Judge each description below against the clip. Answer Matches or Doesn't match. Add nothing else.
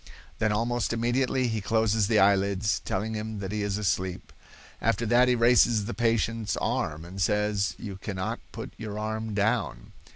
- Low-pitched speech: Matches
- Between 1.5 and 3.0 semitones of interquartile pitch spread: Matches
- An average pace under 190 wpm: Matches